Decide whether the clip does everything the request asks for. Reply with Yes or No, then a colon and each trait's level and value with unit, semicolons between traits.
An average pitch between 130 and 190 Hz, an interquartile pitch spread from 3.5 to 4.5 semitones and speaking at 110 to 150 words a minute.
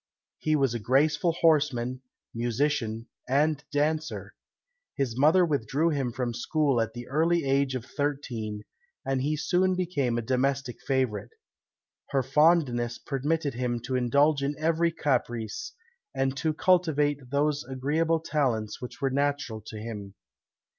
Yes: medium, 140 Hz; average, 4.0 semitones; slow, 135 wpm